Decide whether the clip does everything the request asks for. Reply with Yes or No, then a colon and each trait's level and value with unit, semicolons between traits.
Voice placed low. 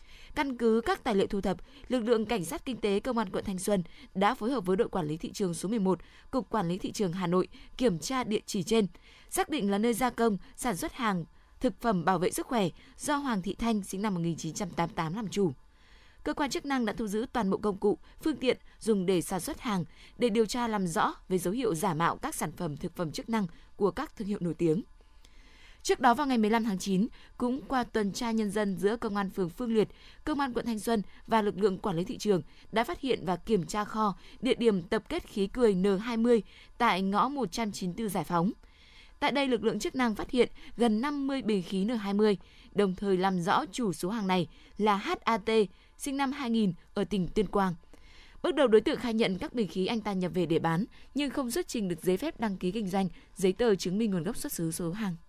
No: high, 215 Hz